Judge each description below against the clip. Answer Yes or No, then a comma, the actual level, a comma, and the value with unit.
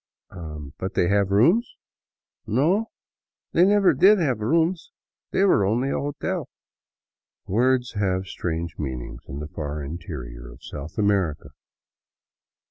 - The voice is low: Yes, low, 100 Hz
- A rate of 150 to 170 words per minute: No, slow, 135 wpm